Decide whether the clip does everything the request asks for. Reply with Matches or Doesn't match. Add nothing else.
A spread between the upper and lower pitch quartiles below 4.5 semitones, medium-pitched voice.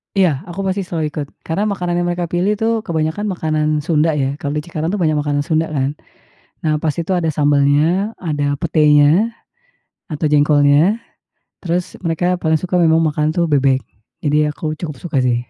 Matches